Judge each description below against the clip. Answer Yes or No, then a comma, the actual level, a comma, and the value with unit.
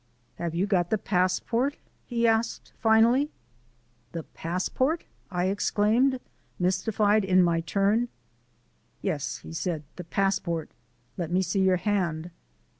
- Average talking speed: No, slow, 120 wpm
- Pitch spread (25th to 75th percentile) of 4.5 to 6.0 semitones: No, average, 4.0 semitones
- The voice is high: Yes, high, 195 Hz